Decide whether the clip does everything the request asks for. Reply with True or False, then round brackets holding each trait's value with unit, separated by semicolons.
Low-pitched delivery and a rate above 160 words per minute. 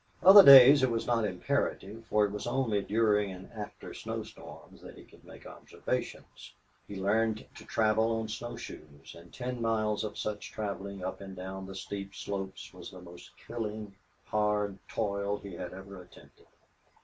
True (105 Hz; 175 wpm)